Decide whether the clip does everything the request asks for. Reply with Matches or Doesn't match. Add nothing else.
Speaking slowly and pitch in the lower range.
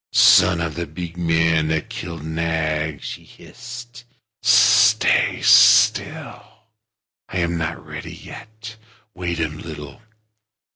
Matches